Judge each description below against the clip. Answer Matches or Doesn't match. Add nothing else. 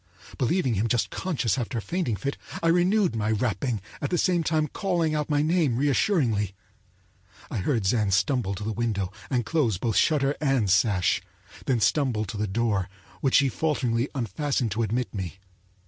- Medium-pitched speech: Doesn't match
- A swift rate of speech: Doesn't match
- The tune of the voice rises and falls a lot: Matches